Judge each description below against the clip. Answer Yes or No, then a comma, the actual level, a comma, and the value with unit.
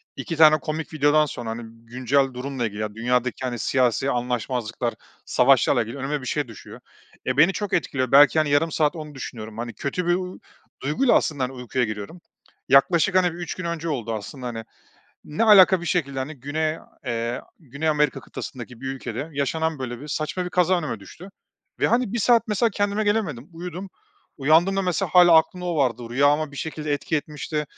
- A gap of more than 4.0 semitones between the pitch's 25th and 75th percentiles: Yes, average, 5.2 semitones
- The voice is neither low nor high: Yes, medium, 145 Hz